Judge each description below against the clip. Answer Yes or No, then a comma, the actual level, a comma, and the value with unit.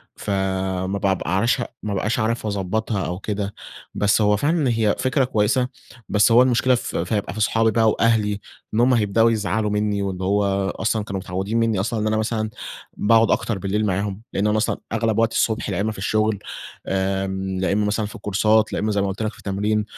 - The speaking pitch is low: Yes, low, 105 Hz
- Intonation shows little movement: Yes, narrow, 2.2 semitones